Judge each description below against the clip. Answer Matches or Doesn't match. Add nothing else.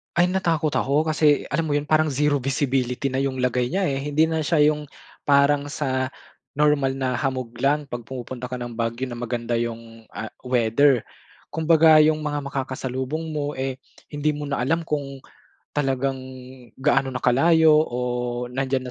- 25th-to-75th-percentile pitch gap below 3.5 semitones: Matches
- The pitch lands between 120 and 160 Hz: Matches